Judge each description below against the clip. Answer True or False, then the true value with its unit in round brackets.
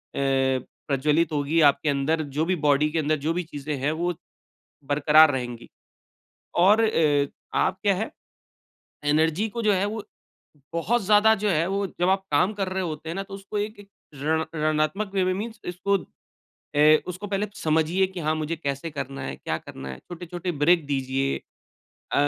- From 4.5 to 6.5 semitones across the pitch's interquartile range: True (4.8 semitones)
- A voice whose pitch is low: False (165 Hz)